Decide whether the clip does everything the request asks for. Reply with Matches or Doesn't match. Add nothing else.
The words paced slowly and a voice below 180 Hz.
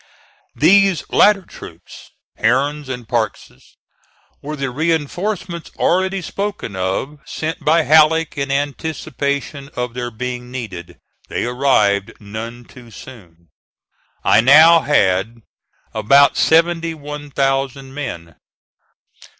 Matches